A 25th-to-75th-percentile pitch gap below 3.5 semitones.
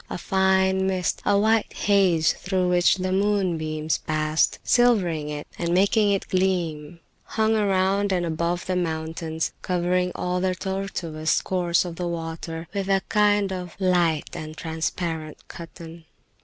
Yes: average, 2.8 semitones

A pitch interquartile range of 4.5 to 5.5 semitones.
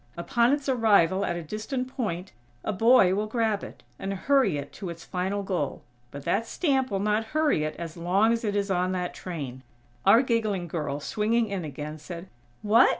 Yes: average, 4.9 semitones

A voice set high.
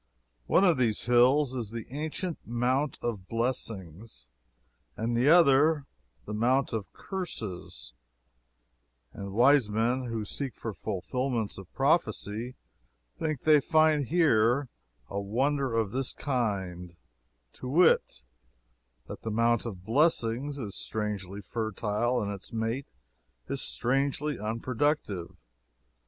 No: low, 120 Hz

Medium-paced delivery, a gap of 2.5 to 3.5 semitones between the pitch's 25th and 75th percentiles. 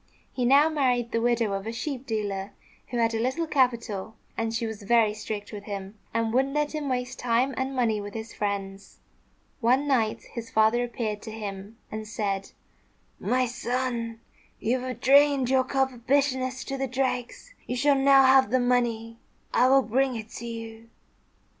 Yes: average, 180 wpm; average, 3.0 semitones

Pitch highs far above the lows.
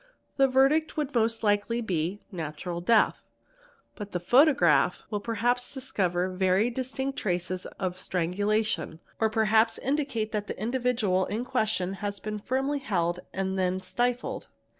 No: average, 5.0 semitones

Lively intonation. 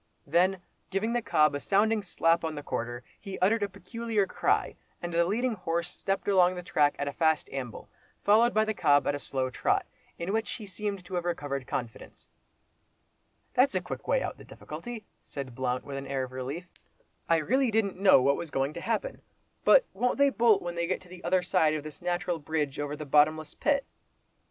Yes: wide, 6.0 semitones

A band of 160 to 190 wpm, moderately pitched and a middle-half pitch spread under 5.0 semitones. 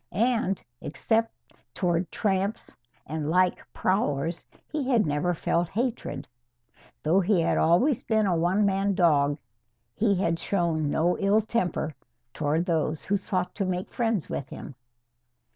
No: average, 140 wpm; medium, 180 Hz; average, 4.1 semitones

